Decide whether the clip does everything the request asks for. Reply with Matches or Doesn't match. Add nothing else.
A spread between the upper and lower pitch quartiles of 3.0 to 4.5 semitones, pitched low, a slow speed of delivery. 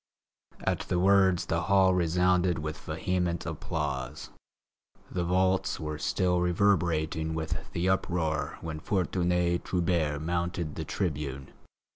Doesn't match